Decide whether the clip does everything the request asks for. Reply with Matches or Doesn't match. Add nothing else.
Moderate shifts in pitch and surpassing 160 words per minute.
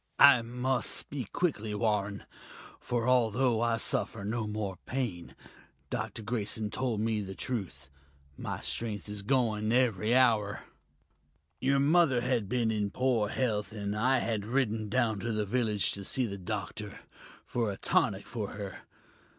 Doesn't match